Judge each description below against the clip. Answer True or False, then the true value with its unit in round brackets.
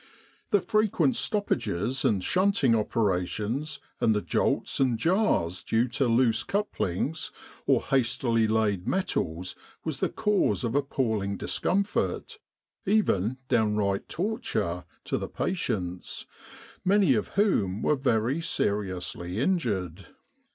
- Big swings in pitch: True (9.0 semitones)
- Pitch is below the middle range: True (115 Hz)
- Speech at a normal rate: False (115 wpm)